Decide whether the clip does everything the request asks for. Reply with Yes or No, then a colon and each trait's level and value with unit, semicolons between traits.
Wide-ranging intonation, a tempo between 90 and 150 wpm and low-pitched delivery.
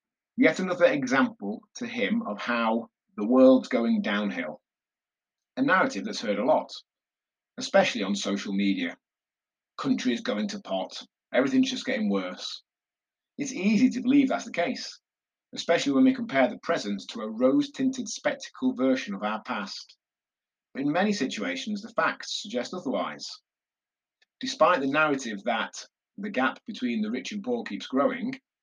No: wide, 5.7 semitones; average, 145 wpm; high, 240 Hz